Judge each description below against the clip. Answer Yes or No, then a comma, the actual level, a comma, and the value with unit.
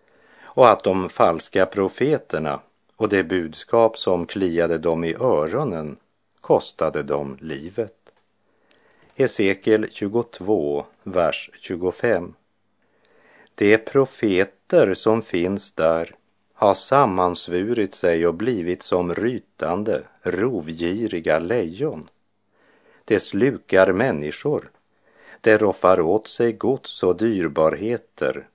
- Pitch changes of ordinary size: Yes, average, 4.9 semitones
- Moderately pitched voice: No, very low, 90 Hz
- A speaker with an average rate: No, slow, 90 wpm